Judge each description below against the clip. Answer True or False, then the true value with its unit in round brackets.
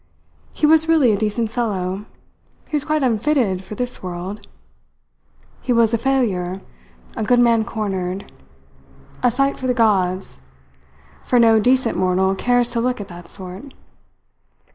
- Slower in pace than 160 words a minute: True (145 wpm)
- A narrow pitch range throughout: False (4.7 semitones)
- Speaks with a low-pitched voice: False (225 Hz)